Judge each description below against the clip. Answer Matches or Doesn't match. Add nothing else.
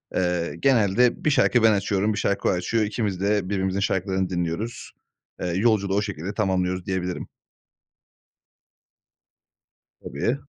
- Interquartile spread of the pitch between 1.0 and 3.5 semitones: Matches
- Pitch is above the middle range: Doesn't match